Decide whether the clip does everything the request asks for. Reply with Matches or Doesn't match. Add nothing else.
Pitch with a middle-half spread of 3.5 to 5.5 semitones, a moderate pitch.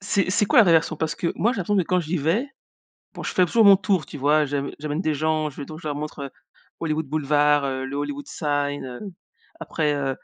Matches